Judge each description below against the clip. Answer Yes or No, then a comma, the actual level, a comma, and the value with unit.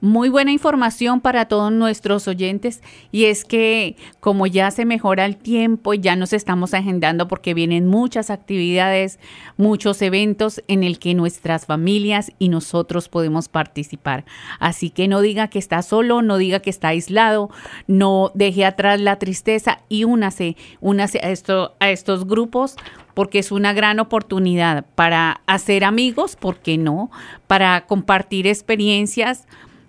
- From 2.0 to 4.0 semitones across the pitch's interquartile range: Yes, average, 3.0 semitones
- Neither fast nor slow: Yes, average, 150 wpm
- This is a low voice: No, high, 195 Hz